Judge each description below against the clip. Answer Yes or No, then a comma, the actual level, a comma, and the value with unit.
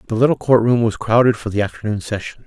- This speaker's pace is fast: Yes, fast, 245 wpm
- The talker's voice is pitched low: Yes, low, 115 Hz